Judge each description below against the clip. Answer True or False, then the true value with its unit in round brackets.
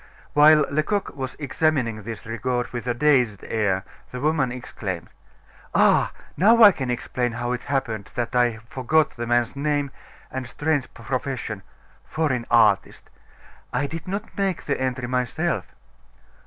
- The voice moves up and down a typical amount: True (4.1 semitones)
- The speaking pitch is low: True (125 Hz)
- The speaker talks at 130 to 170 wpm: True (140 wpm)